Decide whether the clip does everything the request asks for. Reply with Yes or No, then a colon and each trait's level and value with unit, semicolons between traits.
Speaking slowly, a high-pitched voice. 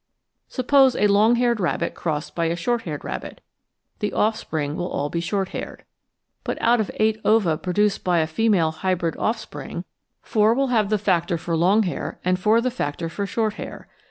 No: average, 185 wpm; high, 195 Hz